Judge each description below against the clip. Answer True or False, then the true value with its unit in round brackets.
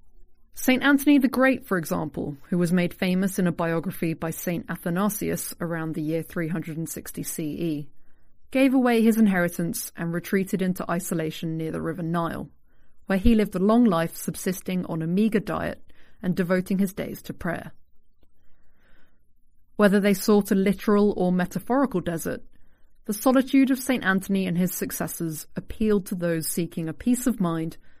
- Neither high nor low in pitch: True (180 Hz)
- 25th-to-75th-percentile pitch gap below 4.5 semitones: True (4.1 semitones)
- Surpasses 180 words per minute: False (160 wpm)